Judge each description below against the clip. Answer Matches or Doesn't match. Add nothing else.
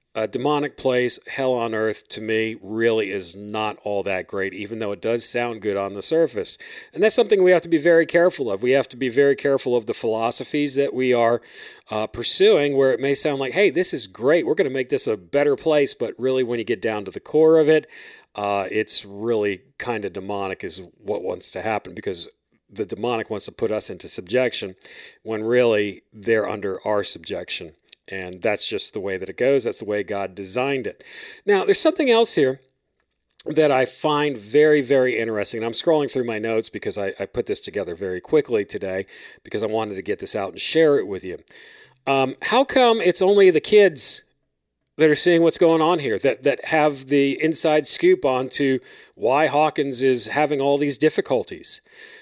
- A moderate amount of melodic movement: Doesn't match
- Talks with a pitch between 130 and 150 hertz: Matches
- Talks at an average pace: Doesn't match